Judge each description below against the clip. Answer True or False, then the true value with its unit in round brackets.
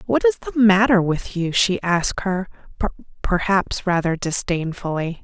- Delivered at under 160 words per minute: True (140 wpm)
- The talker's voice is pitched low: False (185 Hz)